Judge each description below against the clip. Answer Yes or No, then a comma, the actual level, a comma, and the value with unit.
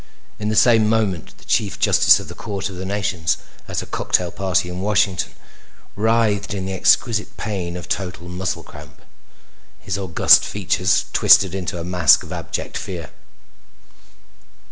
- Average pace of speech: Yes, average, 155 wpm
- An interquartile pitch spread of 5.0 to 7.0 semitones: No, average, 2.7 semitones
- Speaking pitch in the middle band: No, very low, 95 Hz